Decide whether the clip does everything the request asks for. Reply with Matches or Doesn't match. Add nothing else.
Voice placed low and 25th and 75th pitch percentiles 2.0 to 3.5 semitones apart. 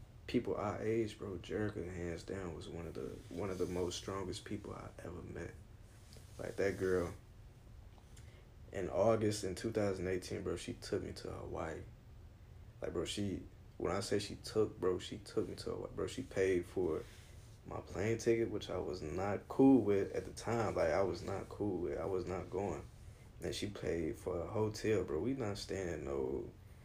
Matches